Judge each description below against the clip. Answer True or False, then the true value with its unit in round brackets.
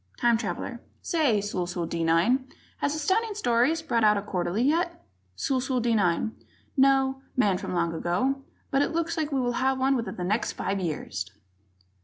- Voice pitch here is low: False (245 Hz)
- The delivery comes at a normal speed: True (175 wpm)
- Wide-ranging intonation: True (6.5 semitones)